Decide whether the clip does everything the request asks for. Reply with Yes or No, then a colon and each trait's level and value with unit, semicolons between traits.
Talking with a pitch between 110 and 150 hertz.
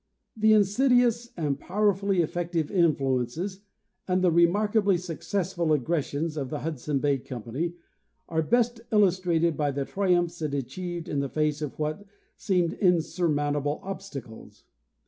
No: medium, 170 Hz